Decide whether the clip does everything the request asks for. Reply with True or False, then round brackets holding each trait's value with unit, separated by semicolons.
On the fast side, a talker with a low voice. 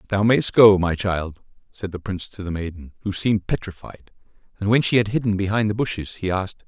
True (215 wpm; 100 Hz)